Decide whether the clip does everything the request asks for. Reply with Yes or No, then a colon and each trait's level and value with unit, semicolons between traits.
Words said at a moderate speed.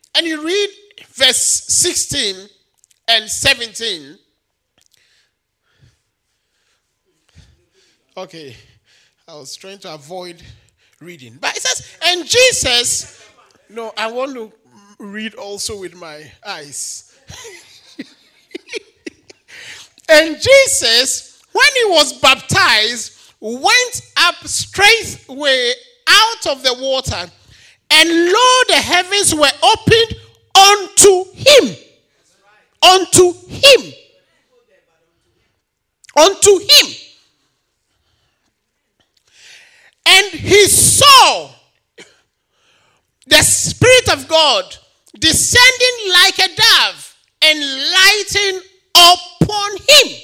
No: slow, 80 wpm